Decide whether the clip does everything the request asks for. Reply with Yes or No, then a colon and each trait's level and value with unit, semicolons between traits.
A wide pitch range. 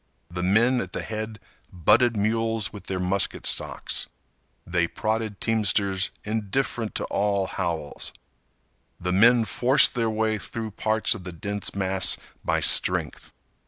No: average, 2.9 semitones